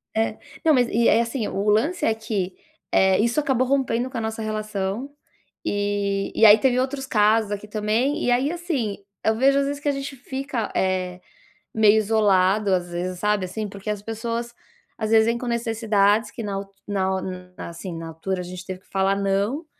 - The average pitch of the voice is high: Yes, high, 215 Hz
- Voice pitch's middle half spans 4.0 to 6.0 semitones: No, average, 3.4 semitones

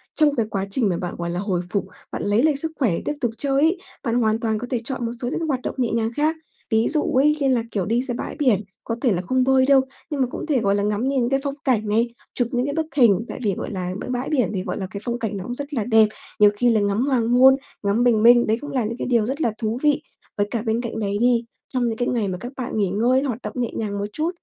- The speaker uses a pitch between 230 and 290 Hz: Yes, high, 235 Hz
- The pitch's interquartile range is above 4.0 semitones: No, average, 3.7 semitones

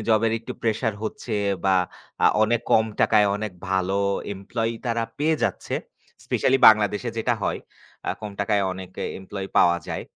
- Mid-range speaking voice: No, low, 110 Hz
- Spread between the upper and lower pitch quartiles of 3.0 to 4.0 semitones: No, narrow, 2.6 semitones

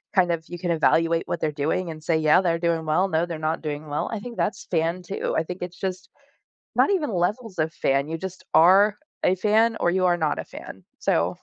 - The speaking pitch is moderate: Yes, medium, 175 Hz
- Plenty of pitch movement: No, average, 2.9 semitones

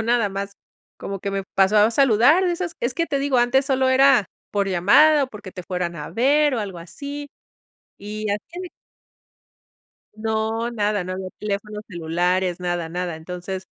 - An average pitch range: No, wide, 5.9 semitones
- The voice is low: No, high, 210 Hz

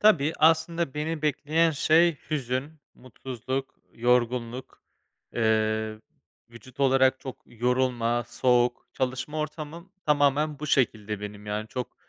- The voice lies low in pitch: Yes, low, 130 Hz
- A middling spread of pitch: Yes, average, 4.1 semitones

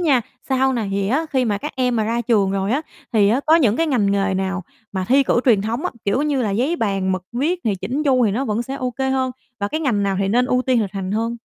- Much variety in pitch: No, average, 4.8 semitones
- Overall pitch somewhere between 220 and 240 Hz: Yes, high, 235 Hz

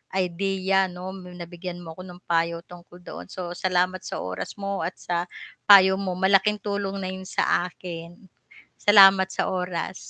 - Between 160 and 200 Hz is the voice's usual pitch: Yes, medium, 185 Hz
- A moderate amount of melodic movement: No, narrow, 1.7 semitones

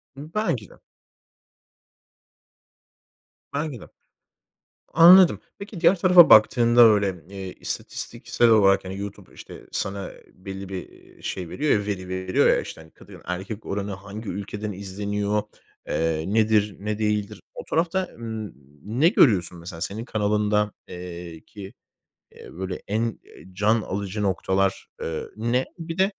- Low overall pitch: Yes, low, 105 Hz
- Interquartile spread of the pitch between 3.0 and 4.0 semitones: Yes, average, 3.4 semitones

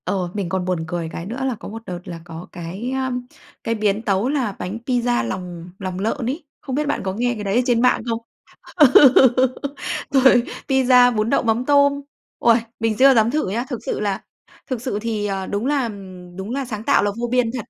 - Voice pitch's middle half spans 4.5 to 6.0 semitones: Yes, average, 4.8 semitones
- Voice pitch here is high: Yes, high, 225 Hz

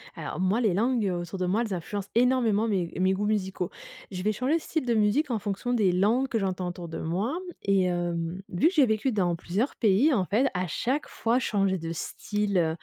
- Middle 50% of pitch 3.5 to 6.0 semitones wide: Yes, average, 4.4 semitones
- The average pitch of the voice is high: Yes, high, 200 Hz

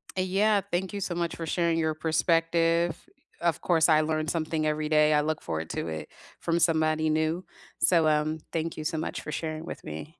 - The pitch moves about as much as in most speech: No, narrow, 1.5 semitones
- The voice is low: No, medium, 160 Hz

